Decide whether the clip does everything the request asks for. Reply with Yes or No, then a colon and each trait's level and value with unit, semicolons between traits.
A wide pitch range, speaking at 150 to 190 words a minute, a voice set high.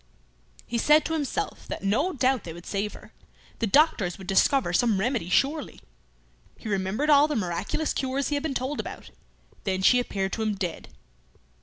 Yes: wide, 6.8 semitones; average, 180 wpm; high, 240 Hz